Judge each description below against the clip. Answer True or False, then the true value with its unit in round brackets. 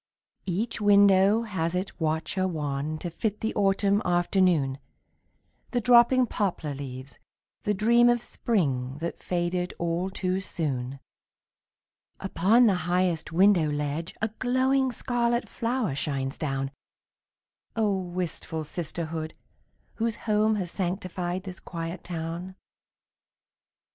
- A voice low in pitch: False (180 Hz)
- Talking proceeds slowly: True (115 wpm)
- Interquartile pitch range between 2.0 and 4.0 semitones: False (4.6 semitones)